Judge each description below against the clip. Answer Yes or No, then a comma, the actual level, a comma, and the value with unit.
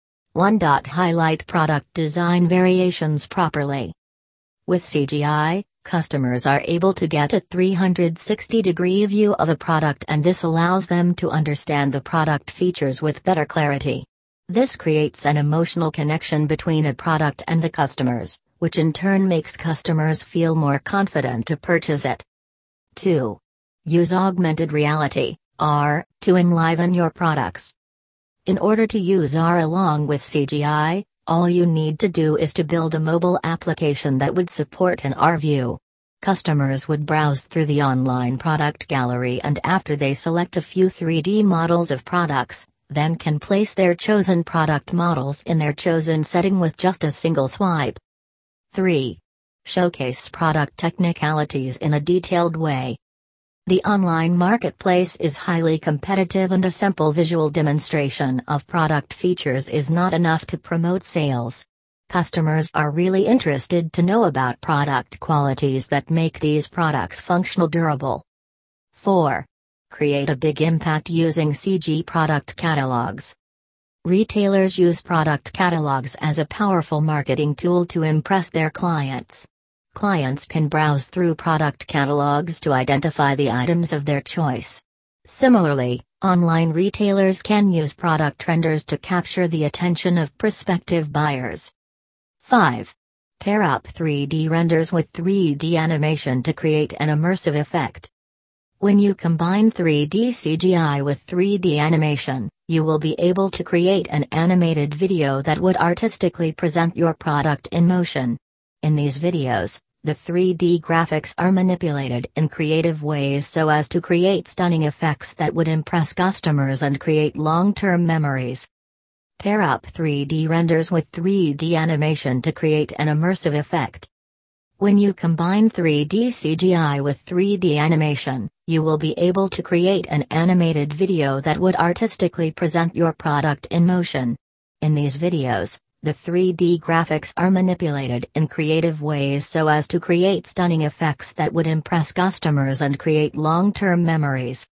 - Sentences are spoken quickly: No, average, 140 wpm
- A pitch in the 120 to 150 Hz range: No, medium, 160 Hz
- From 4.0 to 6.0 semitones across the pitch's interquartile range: No, average, 3.3 semitones